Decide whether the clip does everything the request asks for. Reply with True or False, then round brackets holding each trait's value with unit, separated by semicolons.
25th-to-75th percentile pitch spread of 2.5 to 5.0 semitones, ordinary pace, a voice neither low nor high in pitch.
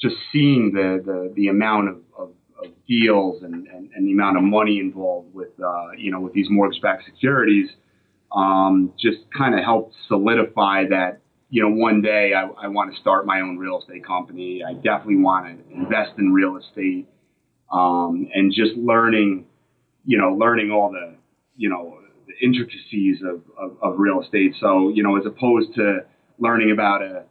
False (3.4 semitones; 180 wpm; 100 Hz)